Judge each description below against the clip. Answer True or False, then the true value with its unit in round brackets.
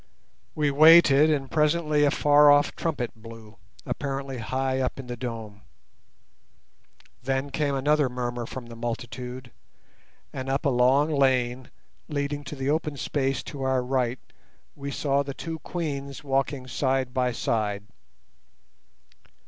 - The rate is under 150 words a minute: True (135 wpm)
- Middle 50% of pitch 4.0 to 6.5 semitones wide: False (2.6 semitones)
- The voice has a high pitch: False (135 Hz)